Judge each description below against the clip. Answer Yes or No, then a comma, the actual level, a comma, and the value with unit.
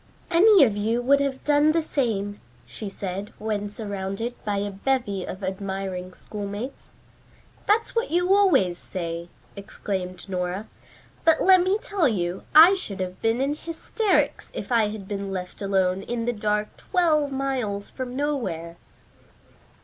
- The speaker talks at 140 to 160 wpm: Yes, average, 150 wpm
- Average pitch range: No, wide, 6.6 semitones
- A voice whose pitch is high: Yes, high, 210 Hz